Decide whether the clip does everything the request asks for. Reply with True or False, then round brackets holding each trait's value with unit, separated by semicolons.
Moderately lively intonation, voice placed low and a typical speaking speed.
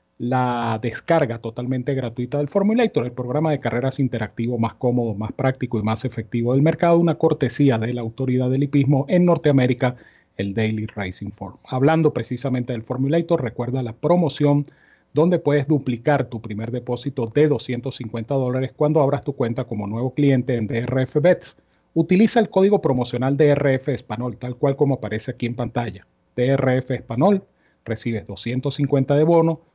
True (3.5 semitones; 130 Hz; 155 wpm)